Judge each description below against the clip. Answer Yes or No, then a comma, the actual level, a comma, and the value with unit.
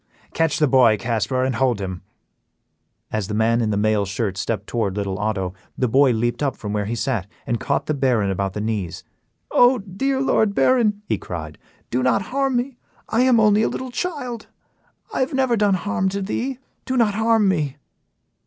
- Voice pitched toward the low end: Yes, low, 130 Hz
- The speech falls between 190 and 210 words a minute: Yes, average, 195 wpm